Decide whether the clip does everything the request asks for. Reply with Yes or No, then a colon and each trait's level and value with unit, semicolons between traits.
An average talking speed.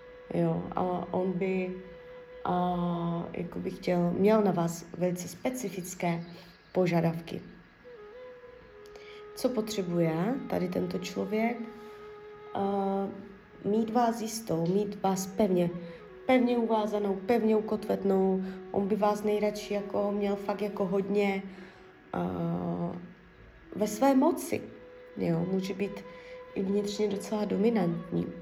No: slow, 105 wpm